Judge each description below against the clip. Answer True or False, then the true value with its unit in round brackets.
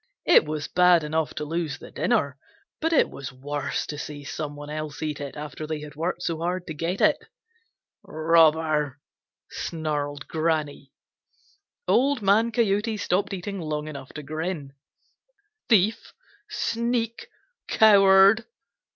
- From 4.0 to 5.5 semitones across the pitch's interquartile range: True (4.8 semitones)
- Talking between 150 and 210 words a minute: False (135 wpm)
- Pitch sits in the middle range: True (160 Hz)